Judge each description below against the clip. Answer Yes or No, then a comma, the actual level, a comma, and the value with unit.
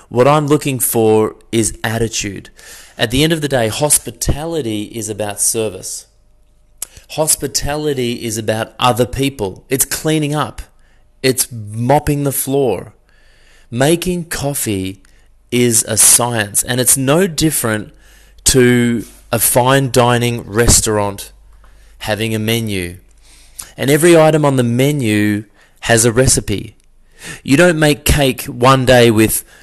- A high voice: No, low, 120 Hz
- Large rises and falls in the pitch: No, average, 4.3 semitones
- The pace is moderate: No, slow, 125 wpm